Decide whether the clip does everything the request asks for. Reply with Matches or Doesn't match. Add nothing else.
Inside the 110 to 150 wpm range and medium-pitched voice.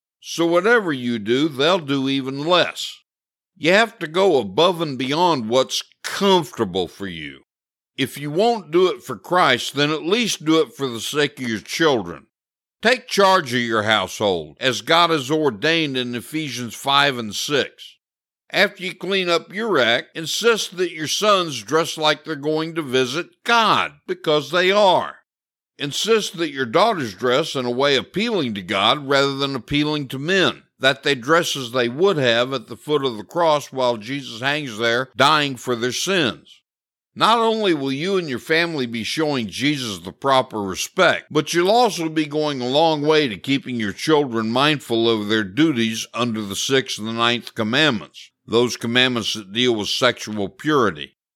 Doesn't match